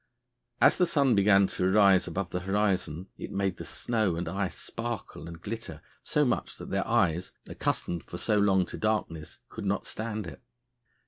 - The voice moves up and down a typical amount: Yes, average, 3.3 semitones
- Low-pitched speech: Yes, low, 100 Hz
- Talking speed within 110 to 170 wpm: No, average, 180 wpm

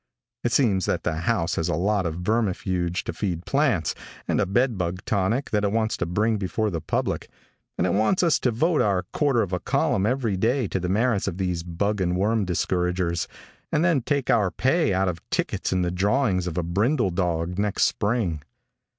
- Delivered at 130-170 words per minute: No, average, 200 wpm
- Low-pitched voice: Yes, low, 100 Hz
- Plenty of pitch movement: No, average, 4.4 semitones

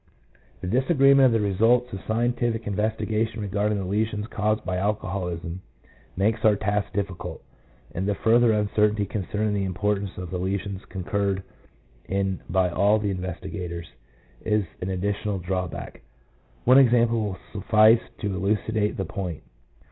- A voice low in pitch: Yes, low, 105 Hz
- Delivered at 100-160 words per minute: Yes, average, 145 wpm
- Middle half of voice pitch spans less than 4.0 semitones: Yes, narrow, 2.6 semitones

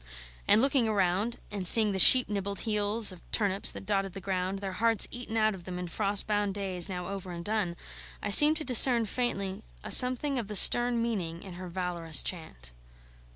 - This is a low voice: No, high, 200 Hz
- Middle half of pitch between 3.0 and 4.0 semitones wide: Yes, average, 3.5 semitones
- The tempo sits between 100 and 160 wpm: No, average, 200 wpm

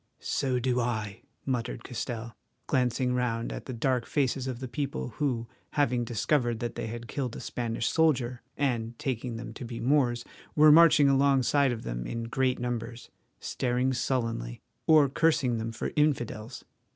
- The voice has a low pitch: Yes, low, 125 Hz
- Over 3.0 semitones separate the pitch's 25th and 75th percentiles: No, narrow, 2.5 semitones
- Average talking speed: Yes, average, 160 wpm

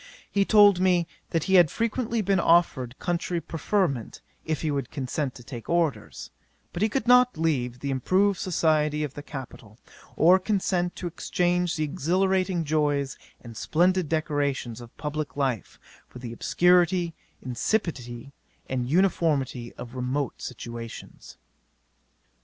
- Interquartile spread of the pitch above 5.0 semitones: Yes, wide, 5.6 semitones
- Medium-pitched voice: Yes, medium, 155 Hz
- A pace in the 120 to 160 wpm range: Yes, slow, 135 wpm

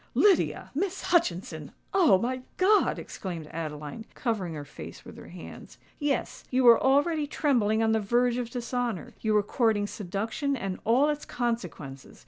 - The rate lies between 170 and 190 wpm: No, average, 140 wpm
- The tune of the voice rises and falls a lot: Yes, wide, 6.3 semitones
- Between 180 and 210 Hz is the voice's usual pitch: No, high, 230 Hz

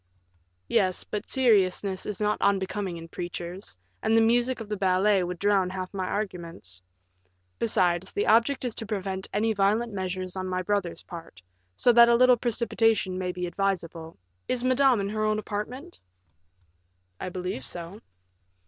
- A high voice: Yes, high, 195 Hz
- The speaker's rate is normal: Yes, average, 155 wpm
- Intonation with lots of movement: No, average, 3.5 semitones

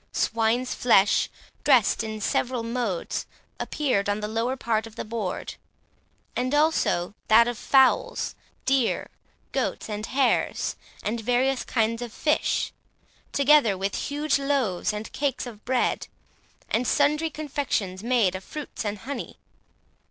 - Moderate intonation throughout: Yes, average, 4.1 semitones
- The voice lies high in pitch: Yes, high, 235 Hz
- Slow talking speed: Yes, slow, 130 wpm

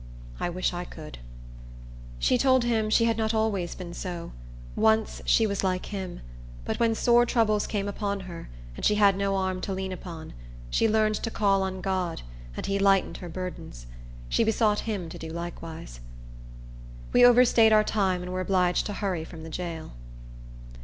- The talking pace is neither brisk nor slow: Yes, average, 180 wpm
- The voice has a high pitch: Yes, high, 195 Hz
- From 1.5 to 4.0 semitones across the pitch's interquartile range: Yes, average, 3.5 semitones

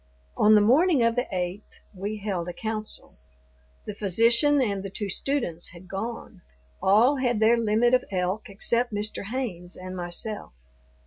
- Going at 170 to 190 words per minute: No, average, 155 wpm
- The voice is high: Yes, high, 210 Hz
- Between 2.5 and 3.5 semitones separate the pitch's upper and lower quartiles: No, average, 3.9 semitones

